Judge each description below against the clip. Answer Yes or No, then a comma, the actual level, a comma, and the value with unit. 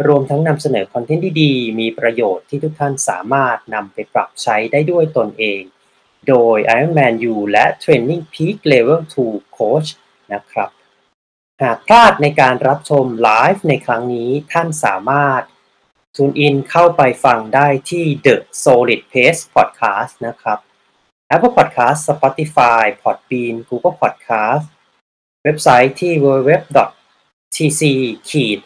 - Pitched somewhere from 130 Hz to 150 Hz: Yes, medium, 140 Hz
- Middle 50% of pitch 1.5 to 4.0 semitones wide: No, average, 4.4 semitones